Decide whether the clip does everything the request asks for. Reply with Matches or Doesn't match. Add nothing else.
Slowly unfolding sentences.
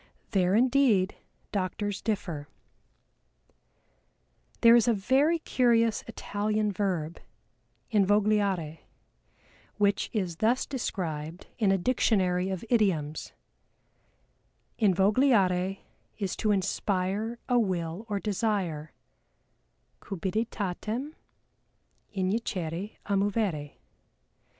Matches